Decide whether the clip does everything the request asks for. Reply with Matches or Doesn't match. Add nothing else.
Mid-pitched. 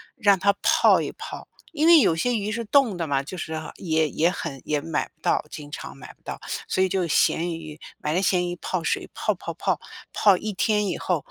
Matches